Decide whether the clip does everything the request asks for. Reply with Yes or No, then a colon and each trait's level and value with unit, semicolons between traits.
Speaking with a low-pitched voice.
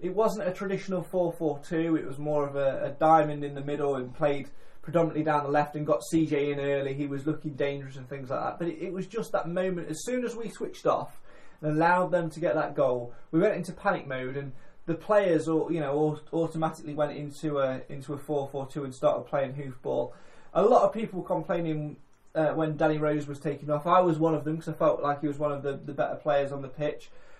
No: medium, 150 Hz